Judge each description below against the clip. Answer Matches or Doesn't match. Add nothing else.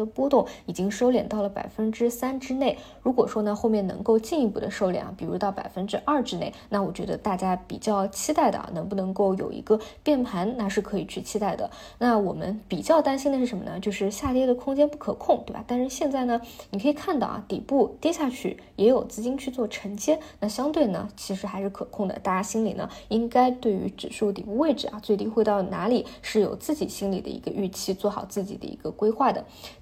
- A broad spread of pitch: Doesn't match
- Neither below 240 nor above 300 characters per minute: Doesn't match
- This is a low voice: Doesn't match